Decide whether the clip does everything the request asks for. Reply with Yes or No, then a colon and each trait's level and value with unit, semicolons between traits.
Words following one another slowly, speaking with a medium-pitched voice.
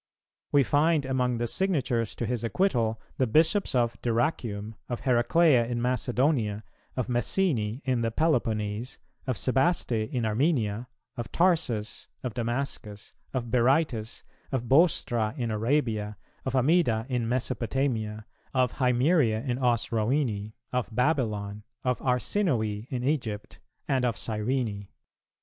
No: slow, 125 wpm; low, 120 Hz